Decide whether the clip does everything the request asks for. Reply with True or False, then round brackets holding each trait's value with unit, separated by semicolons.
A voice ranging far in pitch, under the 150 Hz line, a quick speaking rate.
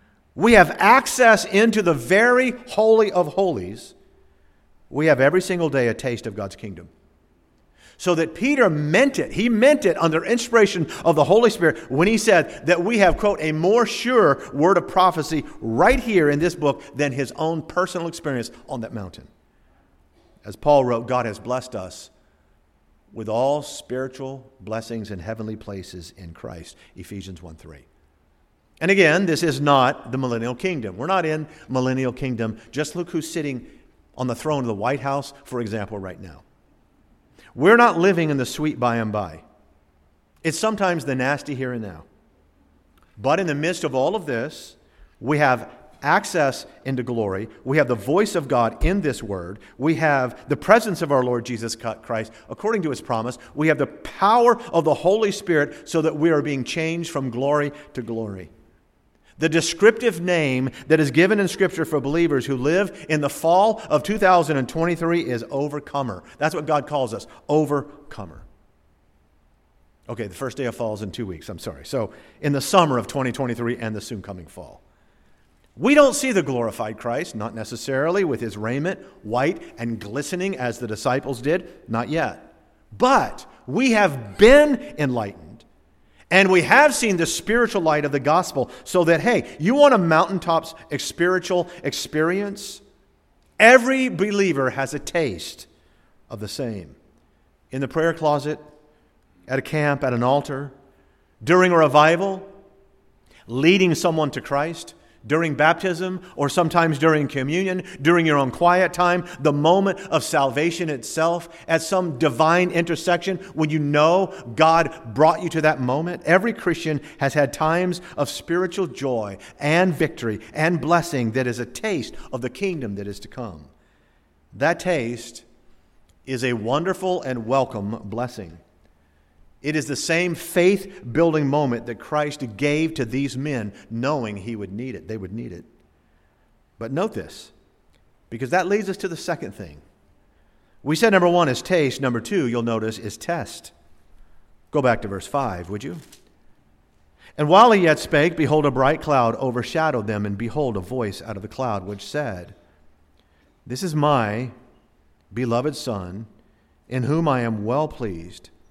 False (7.3 semitones; 140 Hz; 165 wpm)